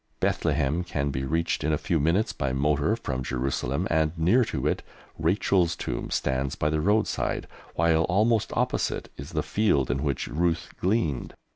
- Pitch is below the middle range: Yes, very low, 80 Hz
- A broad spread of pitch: No, average, 4.5 semitones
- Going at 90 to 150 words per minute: No, average, 165 wpm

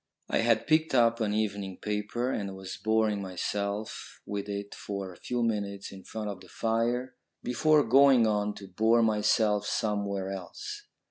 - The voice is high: No, low, 105 Hz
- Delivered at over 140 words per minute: Yes, average, 160 wpm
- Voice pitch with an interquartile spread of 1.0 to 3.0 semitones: Yes, narrow, 2.5 semitones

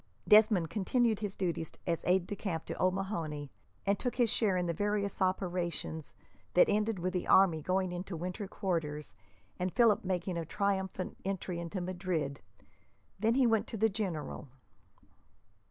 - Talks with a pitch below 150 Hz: No, medium, 185 Hz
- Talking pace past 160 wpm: No, average, 155 wpm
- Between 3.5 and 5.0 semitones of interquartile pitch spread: No, average, 3.1 semitones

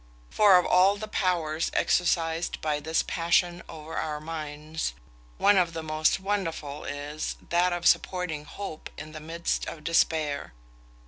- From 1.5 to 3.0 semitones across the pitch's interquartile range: Yes, narrow, 2.6 semitones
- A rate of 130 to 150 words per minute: Yes, average, 145 wpm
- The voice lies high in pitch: No, medium, 165 Hz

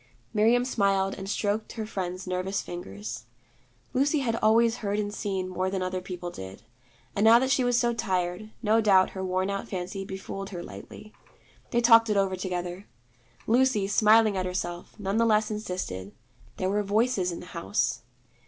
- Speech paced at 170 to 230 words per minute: Yes, average, 175 wpm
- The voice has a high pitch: Yes, high, 195 Hz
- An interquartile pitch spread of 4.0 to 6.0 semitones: No, average, 3.1 semitones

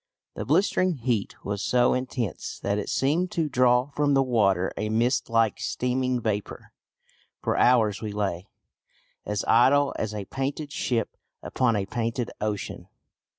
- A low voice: Yes, low, 120 Hz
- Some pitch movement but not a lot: Yes, average, 3.8 semitones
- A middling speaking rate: Yes, average, 150 wpm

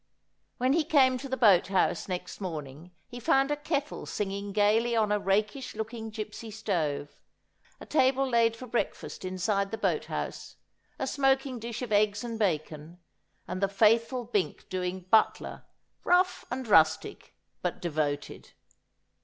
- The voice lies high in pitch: Yes, high, 215 Hz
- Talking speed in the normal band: Yes, average, 150 wpm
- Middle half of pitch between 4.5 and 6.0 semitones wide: Yes, average, 5.1 semitones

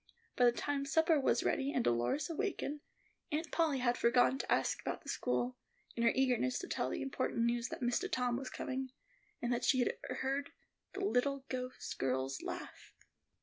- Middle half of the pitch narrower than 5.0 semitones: Yes, average, 2.8 semitones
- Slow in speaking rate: No, average, 185 wpm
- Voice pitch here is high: Yes, very high, 255 Hz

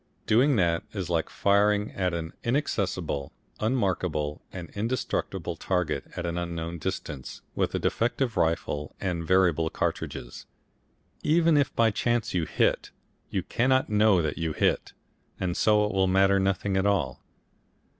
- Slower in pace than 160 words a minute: Yes, average, 145 wpm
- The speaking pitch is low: Yes, very low, 95 Hz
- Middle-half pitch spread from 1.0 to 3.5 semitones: No, average, 4.3 semitones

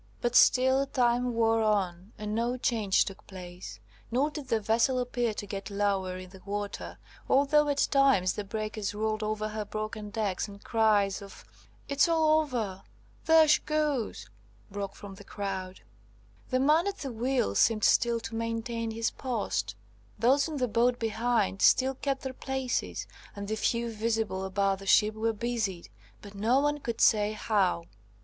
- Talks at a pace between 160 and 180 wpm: Yes, average, 170 wpm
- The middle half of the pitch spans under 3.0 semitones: No, average, 3.9 semitones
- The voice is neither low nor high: No, high, 225 Hz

